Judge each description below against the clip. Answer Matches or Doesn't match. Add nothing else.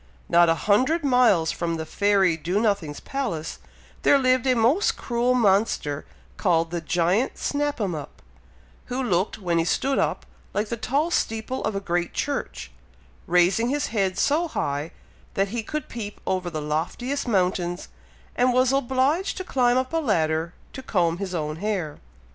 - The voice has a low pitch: Doesn't match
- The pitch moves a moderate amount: Doesn't match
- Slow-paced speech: Doesn't match